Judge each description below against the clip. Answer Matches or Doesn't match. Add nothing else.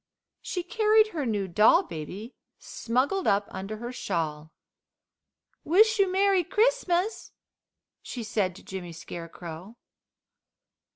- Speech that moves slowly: Matches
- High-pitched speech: Matches